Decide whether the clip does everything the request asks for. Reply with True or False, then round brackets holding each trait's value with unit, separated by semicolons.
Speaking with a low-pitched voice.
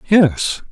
False (170 Hz)